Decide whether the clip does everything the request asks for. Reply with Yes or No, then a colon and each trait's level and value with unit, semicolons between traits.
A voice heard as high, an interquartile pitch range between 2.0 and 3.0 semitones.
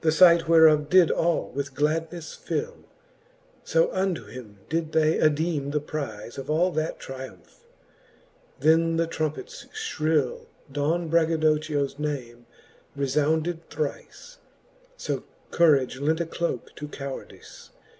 No: medium, 155 Hz; narrow, 2.6 semitones